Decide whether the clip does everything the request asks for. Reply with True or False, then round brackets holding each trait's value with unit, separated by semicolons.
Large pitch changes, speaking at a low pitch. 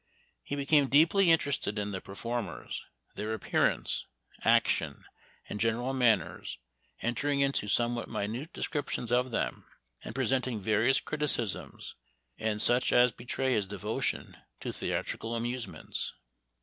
False (3.6 semitones; 120 Hz)